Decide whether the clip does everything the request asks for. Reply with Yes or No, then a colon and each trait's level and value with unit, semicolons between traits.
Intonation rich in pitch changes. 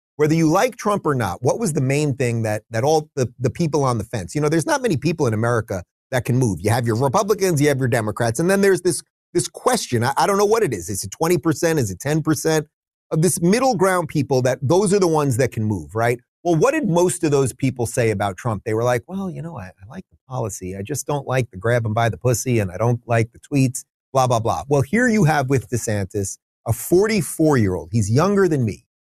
Yes: wide, 6.0 semitones